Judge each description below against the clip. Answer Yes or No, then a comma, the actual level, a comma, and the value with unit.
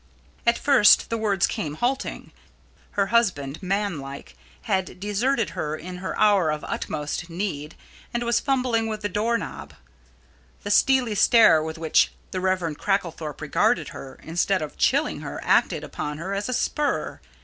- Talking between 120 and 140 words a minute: No, average, 160 wpm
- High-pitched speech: Yes, high, 195 Hz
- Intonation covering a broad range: Yes, wide, 6.1 semitones